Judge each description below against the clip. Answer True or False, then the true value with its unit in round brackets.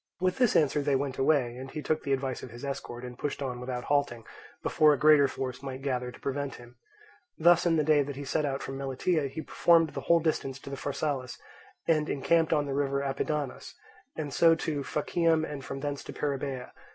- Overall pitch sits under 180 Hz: True (140 Hz)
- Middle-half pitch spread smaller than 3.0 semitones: True (2.5 semitones)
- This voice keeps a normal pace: False (210 wpm)